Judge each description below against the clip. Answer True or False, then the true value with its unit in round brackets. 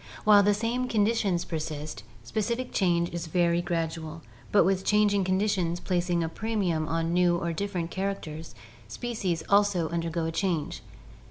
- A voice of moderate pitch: True (175 Hz)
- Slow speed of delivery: False (150 wpm)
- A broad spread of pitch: False (3.6 semitones)